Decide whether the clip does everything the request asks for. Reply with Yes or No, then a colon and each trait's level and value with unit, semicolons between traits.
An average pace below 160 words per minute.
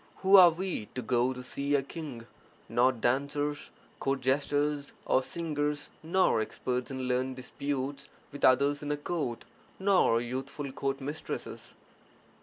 Yes: average, 145 wpm